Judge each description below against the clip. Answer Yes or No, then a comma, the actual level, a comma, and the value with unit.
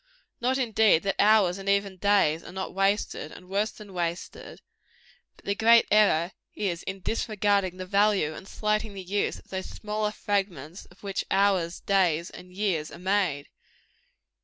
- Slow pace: No, average, 160 wpm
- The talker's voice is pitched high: Yes, high, 195 Hz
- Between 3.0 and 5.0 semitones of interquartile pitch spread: No, narrow, 2.5 semitones